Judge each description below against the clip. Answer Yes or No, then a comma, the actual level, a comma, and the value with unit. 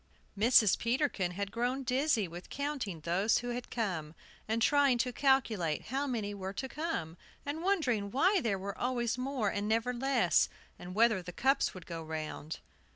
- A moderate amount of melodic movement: No, wide, 5.8 semitones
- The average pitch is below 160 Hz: No, high, 230 Hz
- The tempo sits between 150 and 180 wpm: Yes, average, 170 wpm